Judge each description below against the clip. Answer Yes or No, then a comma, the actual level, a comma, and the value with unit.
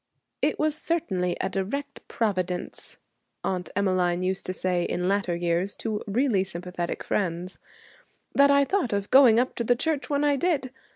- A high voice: Yes, high, 200 Hz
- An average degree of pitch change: No, wide, 7.3 semitones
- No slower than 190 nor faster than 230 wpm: No, average, 165 wpm